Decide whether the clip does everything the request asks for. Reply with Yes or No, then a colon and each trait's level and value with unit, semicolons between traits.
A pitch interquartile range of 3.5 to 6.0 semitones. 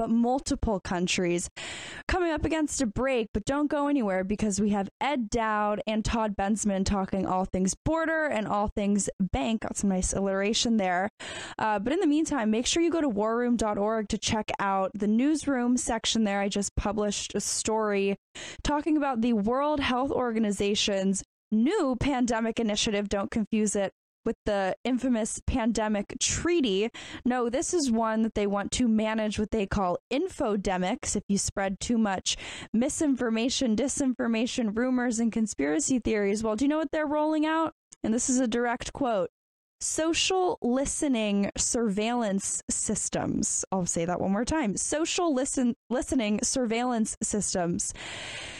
Yes: average, 4.3 semitones